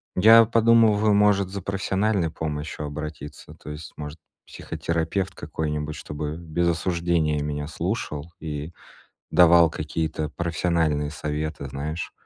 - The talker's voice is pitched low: Yes, very low, 80 Hz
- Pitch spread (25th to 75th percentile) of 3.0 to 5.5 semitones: Yes, average, 3.5 semitones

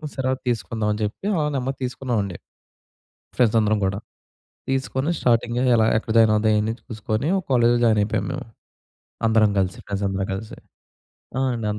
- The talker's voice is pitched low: Yes, low, 110 Hz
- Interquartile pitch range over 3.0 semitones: No, narrow, 2.6 semitones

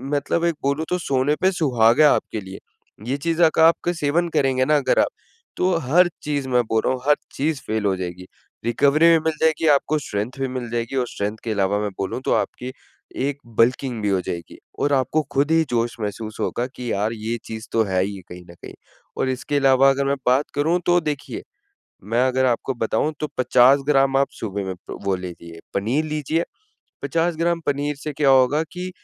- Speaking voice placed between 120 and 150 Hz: Yes, low, 135 Hz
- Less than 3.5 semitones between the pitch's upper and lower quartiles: No, average, 5.2 semitones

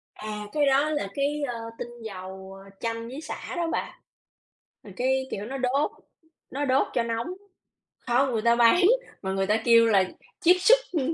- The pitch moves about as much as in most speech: Yes, average, 4.3 semitones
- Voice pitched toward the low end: No, high, 240 Hz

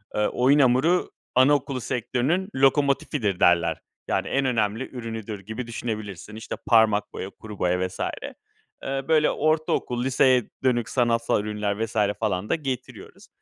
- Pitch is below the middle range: Yes, low, 120 Hz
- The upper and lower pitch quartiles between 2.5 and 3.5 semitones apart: No, average, 4.0 semitones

